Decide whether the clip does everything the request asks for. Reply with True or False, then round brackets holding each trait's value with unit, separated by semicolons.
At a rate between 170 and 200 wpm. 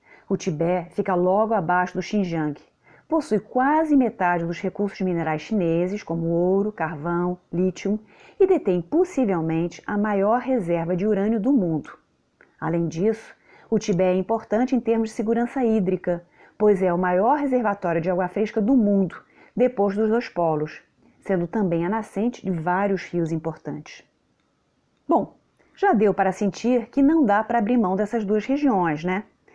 False (155 wpm)